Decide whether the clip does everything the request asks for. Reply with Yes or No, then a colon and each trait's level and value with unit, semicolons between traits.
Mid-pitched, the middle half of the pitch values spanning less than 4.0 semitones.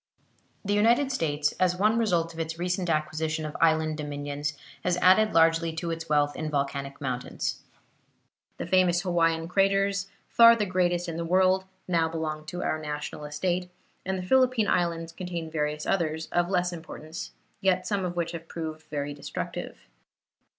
Yes: medium, 165 Hz; average, 2.9 semitones